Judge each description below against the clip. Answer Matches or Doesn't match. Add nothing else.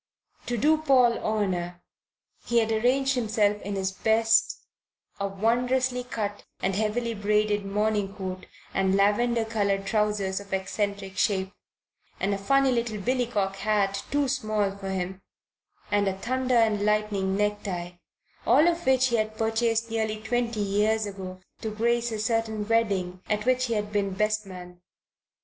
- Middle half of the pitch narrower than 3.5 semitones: Matches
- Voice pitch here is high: Matches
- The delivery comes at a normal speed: Matches